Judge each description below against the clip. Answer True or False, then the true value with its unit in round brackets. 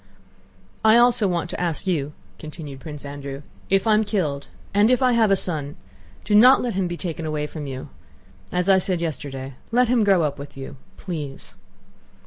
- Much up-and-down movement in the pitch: True (6.3 semitones)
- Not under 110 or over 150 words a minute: False (180 wpm)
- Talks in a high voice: False (170 Hz)